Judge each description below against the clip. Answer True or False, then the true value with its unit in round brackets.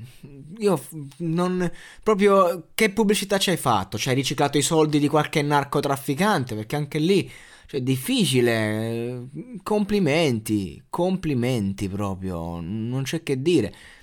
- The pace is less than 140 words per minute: True (130 wpm)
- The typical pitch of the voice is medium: True (145 Hz)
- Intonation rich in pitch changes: True (6.5 semitones)